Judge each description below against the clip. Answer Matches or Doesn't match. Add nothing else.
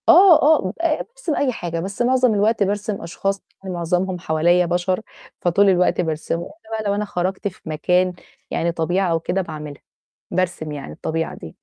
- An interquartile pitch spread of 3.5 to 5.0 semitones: Matches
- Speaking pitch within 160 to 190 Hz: Matches